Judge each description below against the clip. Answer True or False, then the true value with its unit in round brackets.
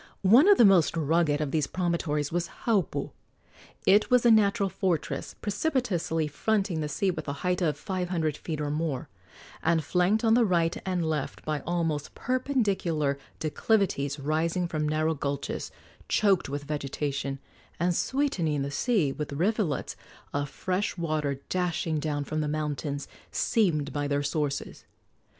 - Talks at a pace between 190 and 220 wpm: False (150 wpm)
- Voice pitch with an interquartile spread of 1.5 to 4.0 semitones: False (4.4 semitones)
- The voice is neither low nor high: True (165 Hz)